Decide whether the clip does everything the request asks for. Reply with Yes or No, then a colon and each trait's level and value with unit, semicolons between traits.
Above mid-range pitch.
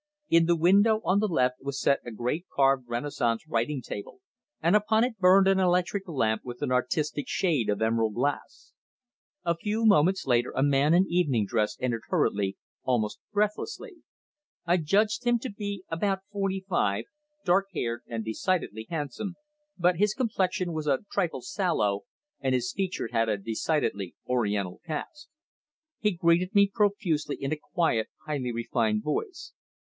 No: medium, 160 Hz